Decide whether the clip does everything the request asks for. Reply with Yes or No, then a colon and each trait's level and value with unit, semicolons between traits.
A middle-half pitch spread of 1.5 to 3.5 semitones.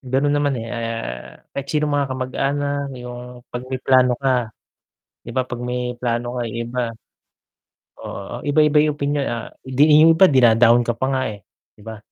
Yes: average, 2.9 semitones